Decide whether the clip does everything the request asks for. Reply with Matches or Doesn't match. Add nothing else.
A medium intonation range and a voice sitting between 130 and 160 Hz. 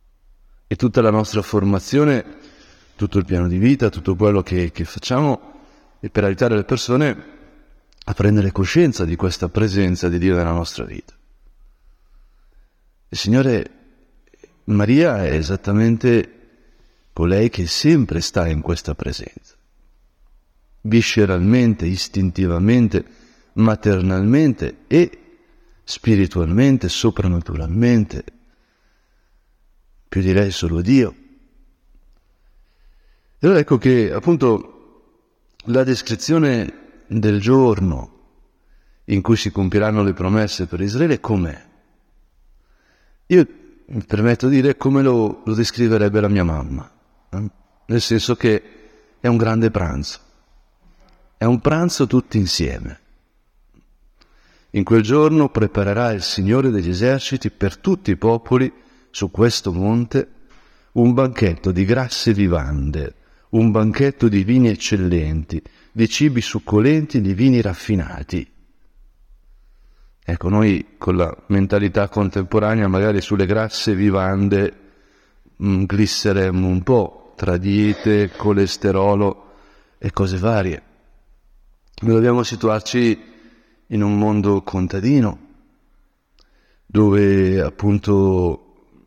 Doesn't match